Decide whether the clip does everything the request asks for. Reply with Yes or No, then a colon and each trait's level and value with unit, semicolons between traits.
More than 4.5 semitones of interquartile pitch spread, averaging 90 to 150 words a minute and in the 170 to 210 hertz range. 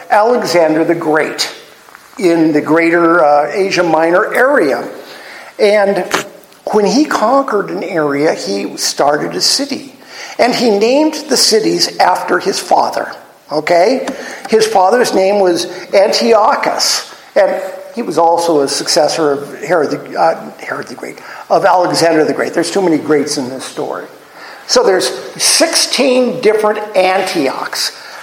Yes: average, 4.9 semitones; slow, 135 wpm; high, 190 Hz